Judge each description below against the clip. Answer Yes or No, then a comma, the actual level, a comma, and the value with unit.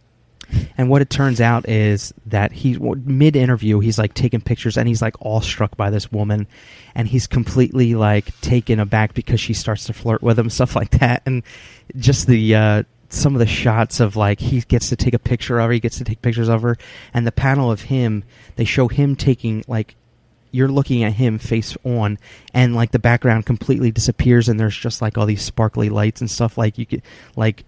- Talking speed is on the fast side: Yes, fast, 210 wpm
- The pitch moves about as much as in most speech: No, narrow, 2.2 semitones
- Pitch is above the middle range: No, low, 115 Hz